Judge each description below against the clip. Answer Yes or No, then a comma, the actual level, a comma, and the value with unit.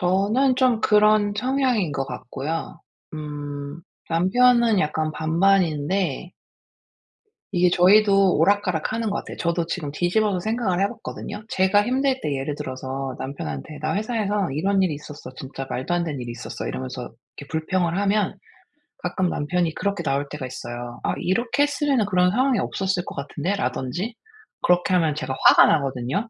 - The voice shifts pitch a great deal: Yes, wide, 6.0 semitones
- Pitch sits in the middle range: Yes, medium, 180 Hz